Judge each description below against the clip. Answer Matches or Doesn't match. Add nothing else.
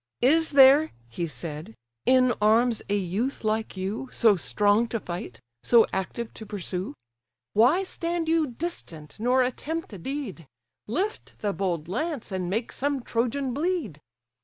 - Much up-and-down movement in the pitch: Matches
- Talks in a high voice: Matches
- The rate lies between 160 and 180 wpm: Doesn't match